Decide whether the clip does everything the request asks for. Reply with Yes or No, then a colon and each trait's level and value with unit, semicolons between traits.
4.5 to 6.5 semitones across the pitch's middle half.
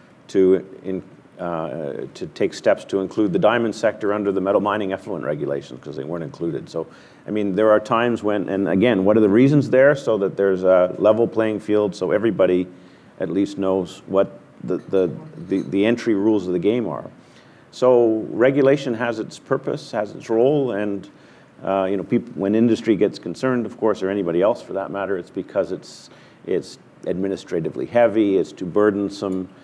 No: average, 2.9 semitones